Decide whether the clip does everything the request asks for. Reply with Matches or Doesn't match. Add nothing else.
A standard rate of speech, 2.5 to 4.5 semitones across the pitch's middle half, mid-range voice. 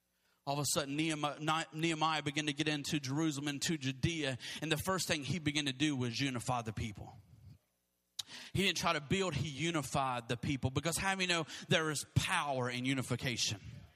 Matches